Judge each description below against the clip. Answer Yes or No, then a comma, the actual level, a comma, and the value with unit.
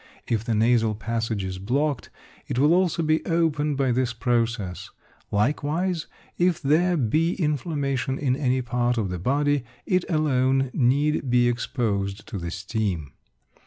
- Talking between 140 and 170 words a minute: Yes, average, 145 wpm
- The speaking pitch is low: Yes, low, 130 Hz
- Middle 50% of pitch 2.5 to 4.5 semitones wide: No, average, 4.9 semitones